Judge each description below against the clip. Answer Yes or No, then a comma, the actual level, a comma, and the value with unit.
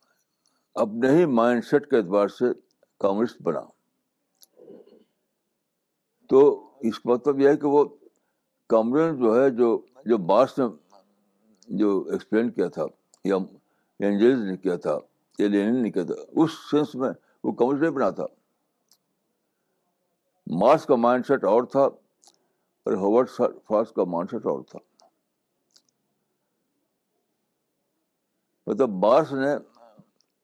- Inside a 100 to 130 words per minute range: Yes, average, 120 wpm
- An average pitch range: No, wide, 5.9 semitones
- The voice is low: Yes, low, 125 Hz